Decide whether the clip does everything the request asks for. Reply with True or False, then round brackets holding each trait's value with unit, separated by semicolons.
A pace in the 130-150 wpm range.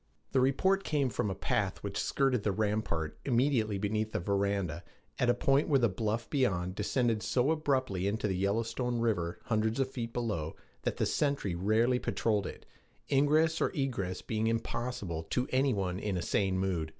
False (175 wpm)